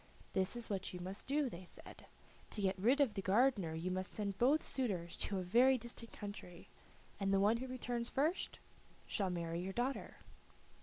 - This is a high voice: Yes, high, 205 Hz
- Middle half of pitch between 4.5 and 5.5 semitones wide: Yes, average, 4.8 semitones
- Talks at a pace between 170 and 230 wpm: Yes, average, 190 wpm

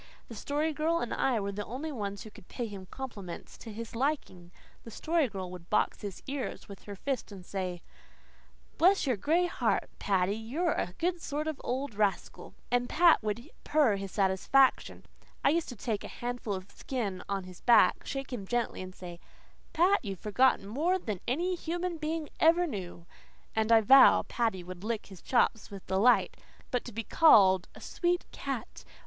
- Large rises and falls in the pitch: Yes, wide, 6.9 semitones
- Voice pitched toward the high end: Yes, high, 230 Hz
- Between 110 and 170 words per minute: No, average, 190 wpm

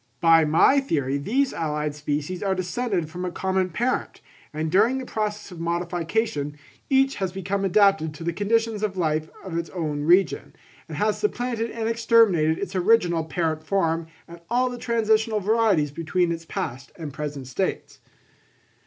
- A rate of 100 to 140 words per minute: No, average, 160 wpm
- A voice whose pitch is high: No, medium, 180 Hz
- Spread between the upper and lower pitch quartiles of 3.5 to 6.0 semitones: Yes, wide, 5.5 semitones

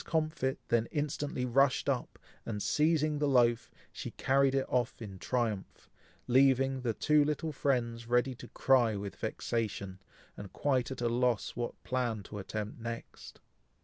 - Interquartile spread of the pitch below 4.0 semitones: Yes, average, 2.9 semitones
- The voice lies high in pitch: No, low, 125 Hz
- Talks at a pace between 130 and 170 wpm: Yes, average, 150 wpm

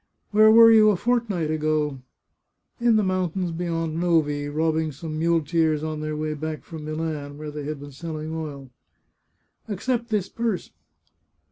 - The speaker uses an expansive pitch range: No, average, 3.5 semitones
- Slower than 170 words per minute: No, average, 175 wpm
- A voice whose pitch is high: No, medium, 160 Hz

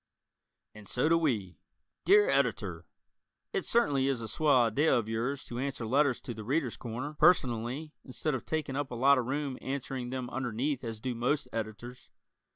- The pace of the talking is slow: No, average, 175 wpm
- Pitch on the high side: No, low, 130 Hz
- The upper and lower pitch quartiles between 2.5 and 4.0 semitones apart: Yes, average, 3.6 semitones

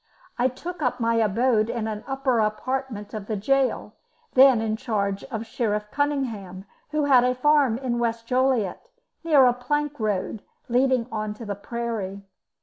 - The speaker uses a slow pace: No, average, 160 wpm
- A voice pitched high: Yes, high, 235 Hz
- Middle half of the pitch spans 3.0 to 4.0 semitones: Yes, average, 3.6 semitones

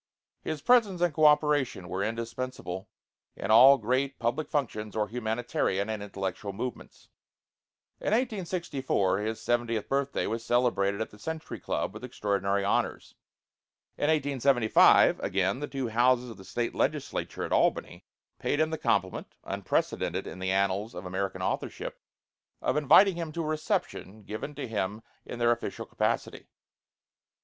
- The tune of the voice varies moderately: No, wide, 6.1 semitones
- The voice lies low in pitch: Yes, low, 120 Hz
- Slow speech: No, average, 145 wpm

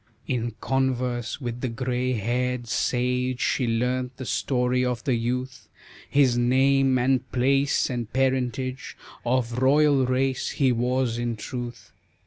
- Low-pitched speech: Yes, low, 125 Hz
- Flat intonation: Yes, narrow, 1.4 semitones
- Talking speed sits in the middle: No, slow, 130 wpm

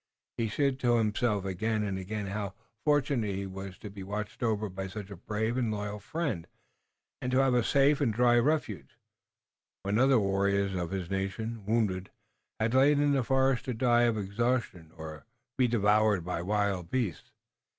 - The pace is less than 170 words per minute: No, average, 180 wpm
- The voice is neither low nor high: No, low, 105 Hz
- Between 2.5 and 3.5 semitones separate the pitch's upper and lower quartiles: No, average, 4.0 semitones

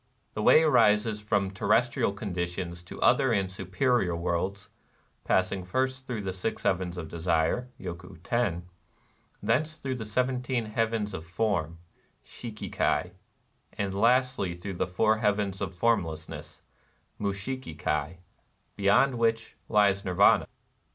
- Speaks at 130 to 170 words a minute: Yes, average, 140 wpm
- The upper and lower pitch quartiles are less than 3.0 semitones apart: No, average, 4.3 semitones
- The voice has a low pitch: Yes, low, 100 Hz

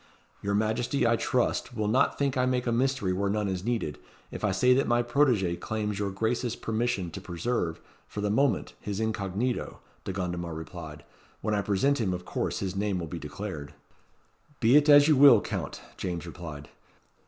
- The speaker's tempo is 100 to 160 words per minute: No, average, 190 wpm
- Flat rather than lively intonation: No, average, 5.0 semitones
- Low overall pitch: Yes, low, 105 Hz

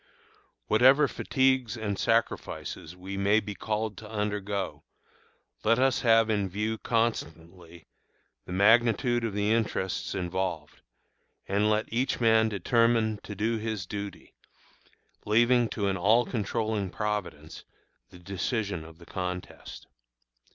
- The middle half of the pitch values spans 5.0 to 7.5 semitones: No, average, 3.0 semitones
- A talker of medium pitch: No, low, 105 Hz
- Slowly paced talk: Yes, slow, 125 wpm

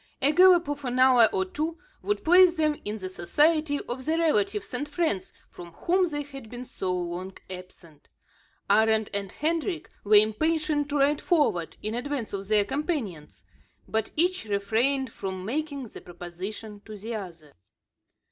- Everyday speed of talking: Yes, average, 160 wpm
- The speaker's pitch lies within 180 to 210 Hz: No, high, 240 Hz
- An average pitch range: No, wide, 7.1 semitones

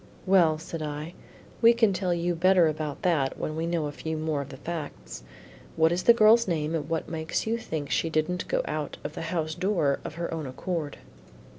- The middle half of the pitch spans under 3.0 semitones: Yes, narrow, 2.6 semitones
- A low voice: No, medium, 160 Hz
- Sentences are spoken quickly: Yes, fast, 210 wpm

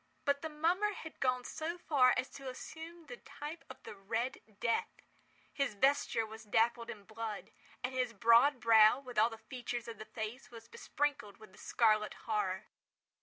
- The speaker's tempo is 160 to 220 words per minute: Yes, average, 170 wpm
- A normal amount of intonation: Yes, average, 4.2 semitones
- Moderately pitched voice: No, high, 240 Hz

